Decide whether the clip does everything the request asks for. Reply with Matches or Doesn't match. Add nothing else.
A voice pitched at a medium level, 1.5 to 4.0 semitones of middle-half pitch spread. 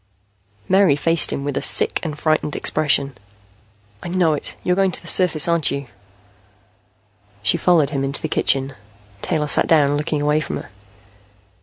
Matches